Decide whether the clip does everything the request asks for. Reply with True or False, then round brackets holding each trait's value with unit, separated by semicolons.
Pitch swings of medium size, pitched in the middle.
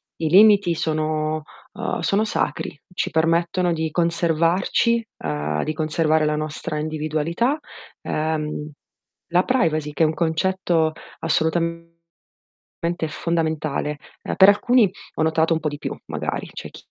False (2.2 semitones; 160 Hz)